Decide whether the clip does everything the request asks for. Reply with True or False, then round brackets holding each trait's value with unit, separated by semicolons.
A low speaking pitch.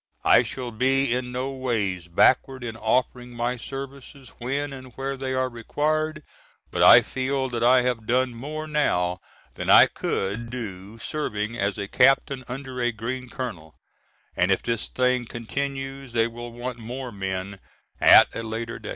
True (125 Hz)